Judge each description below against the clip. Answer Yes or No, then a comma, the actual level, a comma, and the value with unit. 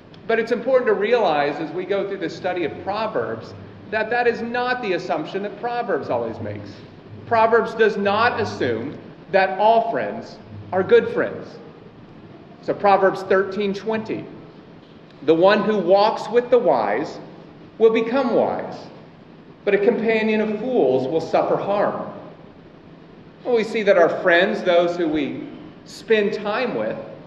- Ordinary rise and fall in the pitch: Yes, average, 4.0 semitones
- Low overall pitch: No, high, 210 Hz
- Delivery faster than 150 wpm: No, average, 145 wpm